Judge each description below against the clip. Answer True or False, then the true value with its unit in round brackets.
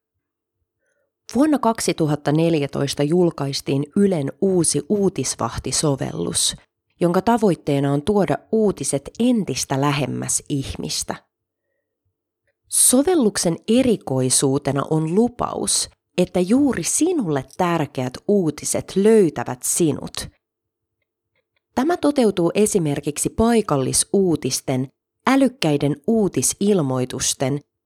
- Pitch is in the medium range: True (155 Hz)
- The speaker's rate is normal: False (65 wpm)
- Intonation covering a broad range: True (7.2 semitones)